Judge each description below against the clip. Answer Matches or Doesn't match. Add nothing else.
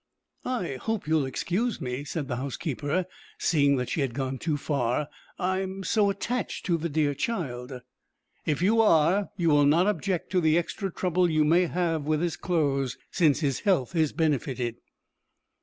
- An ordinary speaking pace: Matches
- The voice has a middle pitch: Matches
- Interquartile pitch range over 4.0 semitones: Matches